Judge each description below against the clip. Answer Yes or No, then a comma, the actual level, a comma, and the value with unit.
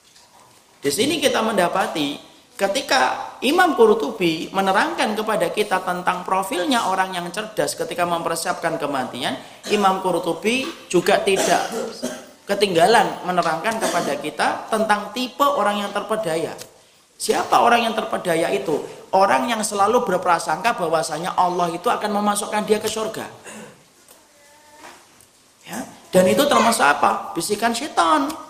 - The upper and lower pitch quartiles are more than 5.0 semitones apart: Yes, wide, 5.4 semitones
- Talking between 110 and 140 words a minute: Yes, average, 115 wpm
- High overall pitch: Yes, high, 210 Hz